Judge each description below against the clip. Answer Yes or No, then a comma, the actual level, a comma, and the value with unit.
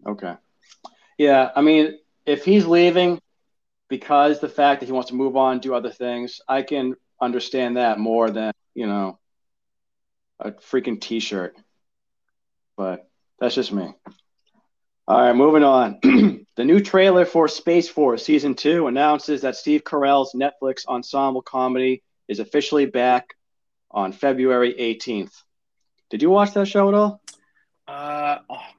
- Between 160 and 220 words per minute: No, average, 145 wpm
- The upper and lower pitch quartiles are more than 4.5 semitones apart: No, average, 3.6 semitones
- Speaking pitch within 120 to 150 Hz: Yes, low, 135 Hz